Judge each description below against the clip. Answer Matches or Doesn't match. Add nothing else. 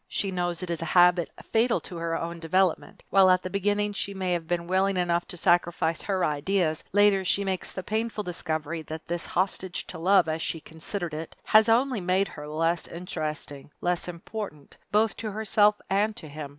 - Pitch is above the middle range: Doesn't match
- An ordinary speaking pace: Matches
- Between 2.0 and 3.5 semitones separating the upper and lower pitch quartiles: Matches